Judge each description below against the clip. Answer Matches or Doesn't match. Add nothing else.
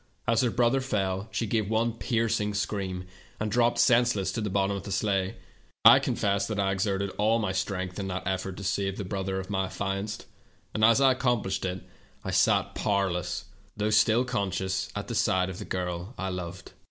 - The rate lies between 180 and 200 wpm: Matches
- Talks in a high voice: Doesn't match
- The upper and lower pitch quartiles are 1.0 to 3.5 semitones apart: Matches